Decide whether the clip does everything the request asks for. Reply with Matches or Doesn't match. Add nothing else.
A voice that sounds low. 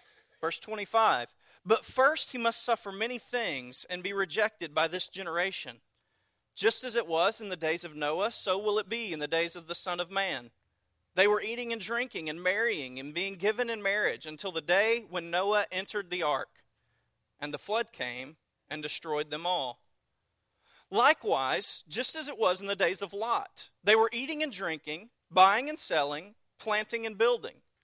Doesn't match